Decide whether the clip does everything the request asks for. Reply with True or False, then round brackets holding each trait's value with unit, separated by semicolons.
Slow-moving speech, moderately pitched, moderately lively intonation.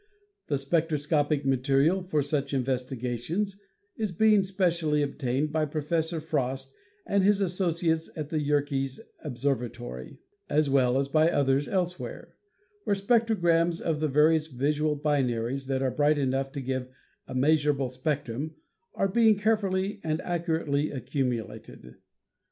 True (130 wpm; 150 Hz; 3.8 semitones)